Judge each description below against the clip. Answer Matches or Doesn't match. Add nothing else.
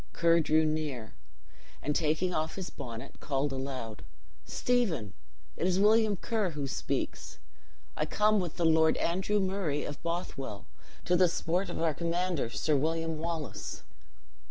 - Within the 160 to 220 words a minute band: Doesn't match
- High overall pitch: Doesn't match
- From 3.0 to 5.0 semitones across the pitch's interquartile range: Matches